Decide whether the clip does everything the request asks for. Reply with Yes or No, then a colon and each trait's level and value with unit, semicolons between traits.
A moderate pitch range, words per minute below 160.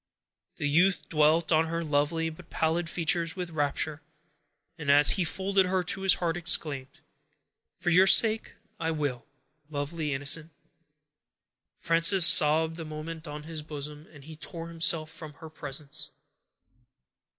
No: narrow, 2.0 semitones; average, 140 wpm